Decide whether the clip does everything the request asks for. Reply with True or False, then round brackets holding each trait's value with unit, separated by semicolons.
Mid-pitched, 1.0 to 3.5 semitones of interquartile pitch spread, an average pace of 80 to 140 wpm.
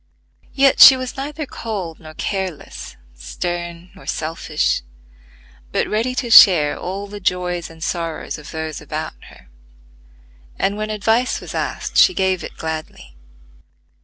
False (180 Hz; 5.1 semitones; 135 wpm)